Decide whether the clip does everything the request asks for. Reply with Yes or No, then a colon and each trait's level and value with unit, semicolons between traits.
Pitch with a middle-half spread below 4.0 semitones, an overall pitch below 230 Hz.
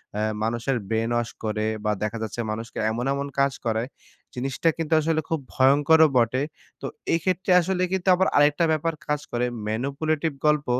No: average, 5.3 semitones; medium, 140 Hz